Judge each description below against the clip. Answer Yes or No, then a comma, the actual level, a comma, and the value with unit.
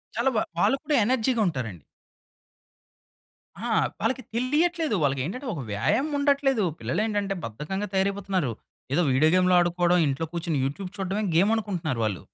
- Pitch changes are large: Yes, wide, 7.0 semitones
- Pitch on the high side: Yes, high, 195 Hz